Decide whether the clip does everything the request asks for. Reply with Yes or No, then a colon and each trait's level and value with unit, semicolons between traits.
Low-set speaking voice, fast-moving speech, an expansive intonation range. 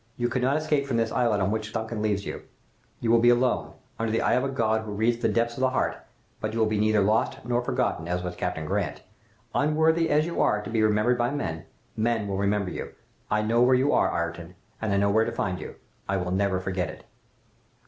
No: low, 110 Hz; fast, 240 wpm; average, 3.4 semitones